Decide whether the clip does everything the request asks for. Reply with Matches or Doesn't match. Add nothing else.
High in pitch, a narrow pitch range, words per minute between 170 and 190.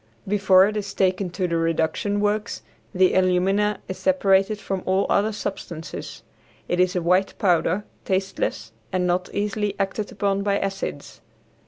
Doesn't match